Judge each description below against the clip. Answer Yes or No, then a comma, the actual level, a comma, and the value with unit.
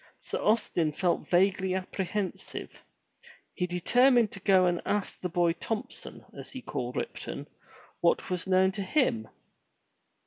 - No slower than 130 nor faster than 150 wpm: Yes, slow, 135 wpm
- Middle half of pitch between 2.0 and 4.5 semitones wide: Yes, average, 2.8 semitones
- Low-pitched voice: No, medium, 185 Hz